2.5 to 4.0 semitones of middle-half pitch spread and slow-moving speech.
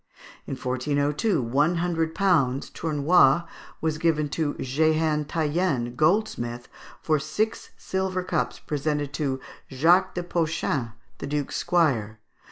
Yes: average, 3.7 semitones; slow, 115 wpm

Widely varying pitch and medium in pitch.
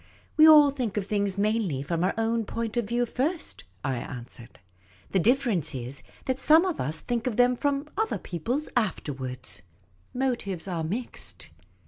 No: wide, 7.8 semitones; high, 220 Hz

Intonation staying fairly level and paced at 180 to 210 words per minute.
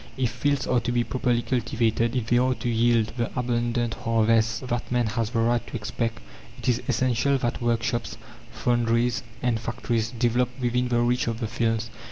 Yes: narrow, 1.1 semitones; average, 185 wpm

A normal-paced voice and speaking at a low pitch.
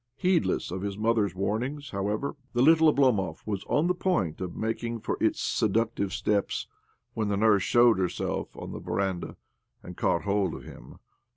Yes: average, 170 wpm; low, 105 Hz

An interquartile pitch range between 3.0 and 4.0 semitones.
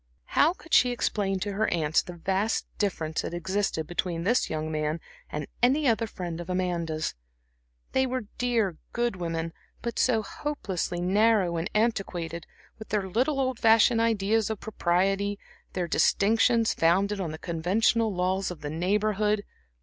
No: average, 4.5 semitones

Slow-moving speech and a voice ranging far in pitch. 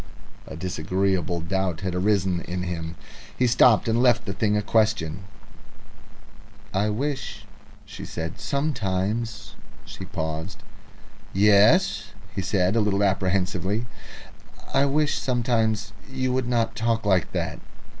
No: slow, 125 wpm; average, 3.9 semitones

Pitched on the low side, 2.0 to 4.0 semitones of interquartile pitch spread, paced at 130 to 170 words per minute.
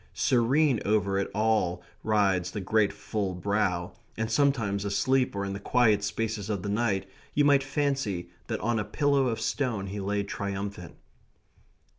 Yes: low, 105 Hz; average, 3.3 semitones; average, 160 wpm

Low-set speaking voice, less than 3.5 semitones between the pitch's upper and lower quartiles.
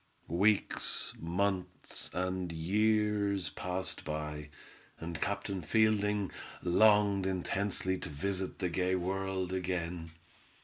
Yes: very low, 95 Hz; narrow, 2.4 semitones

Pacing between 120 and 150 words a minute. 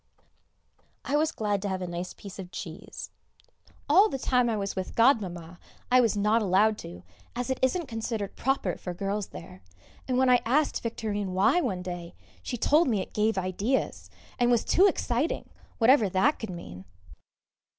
No: average, 175 wpm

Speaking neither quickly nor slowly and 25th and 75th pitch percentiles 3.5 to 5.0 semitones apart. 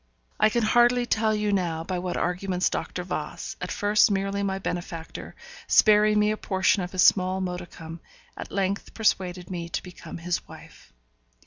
No: average, 165 wpm; average, 2.9 semitones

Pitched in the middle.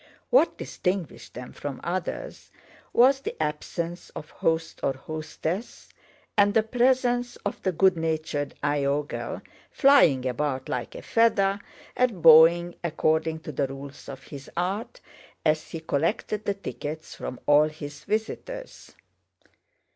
Yes: medium, 165 Hz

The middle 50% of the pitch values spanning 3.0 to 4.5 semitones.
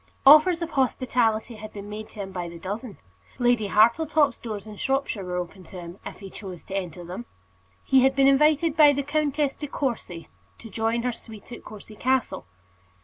No: wide, 5.5 semitones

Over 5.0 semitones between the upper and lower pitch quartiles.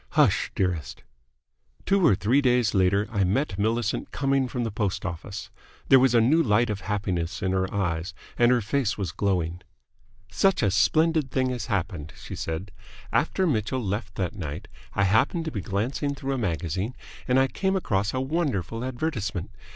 Yes: wide, 5.5 semitones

